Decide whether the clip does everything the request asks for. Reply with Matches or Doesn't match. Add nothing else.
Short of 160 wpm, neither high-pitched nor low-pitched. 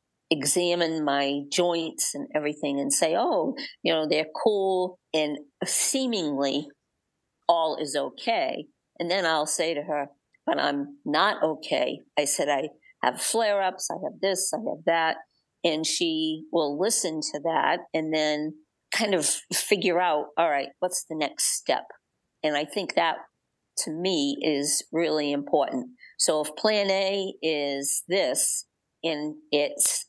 Matches